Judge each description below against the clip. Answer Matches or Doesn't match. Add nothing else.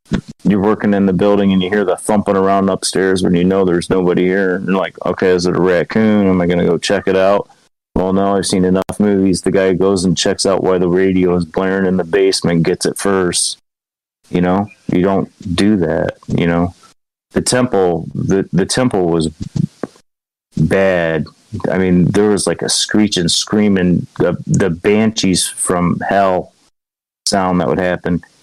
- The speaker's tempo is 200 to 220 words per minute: Doesn't match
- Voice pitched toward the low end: Matches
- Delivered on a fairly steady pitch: Matches